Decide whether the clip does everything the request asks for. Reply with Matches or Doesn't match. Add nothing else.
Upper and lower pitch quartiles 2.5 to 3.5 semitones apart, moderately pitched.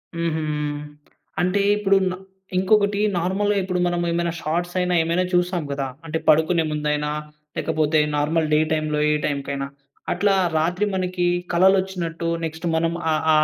Matches